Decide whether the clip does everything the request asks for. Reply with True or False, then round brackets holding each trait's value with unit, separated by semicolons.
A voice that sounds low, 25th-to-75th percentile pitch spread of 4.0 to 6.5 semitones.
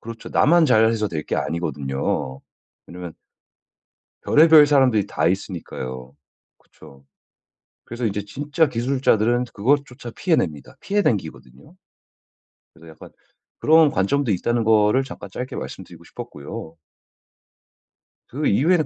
False (115 Hz; 8.3 semitones)